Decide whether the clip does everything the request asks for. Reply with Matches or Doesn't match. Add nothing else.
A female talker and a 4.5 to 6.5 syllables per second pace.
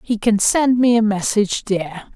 Matches